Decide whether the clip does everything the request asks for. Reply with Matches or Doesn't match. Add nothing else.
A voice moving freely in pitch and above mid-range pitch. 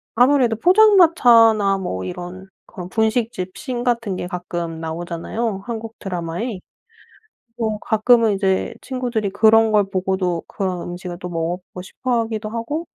Doesn't match